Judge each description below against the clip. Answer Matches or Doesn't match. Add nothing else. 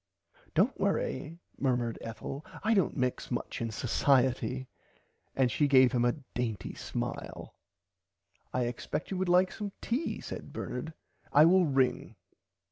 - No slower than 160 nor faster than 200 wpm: Doesn't match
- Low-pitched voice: Matches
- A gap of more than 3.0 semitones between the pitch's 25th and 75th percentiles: Matches